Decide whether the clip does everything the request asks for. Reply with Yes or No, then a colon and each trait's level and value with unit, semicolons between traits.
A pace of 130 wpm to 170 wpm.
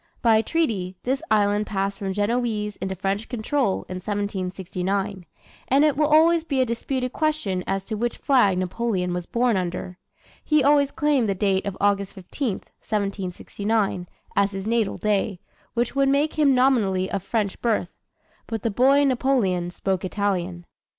Yes: average, 155 wpm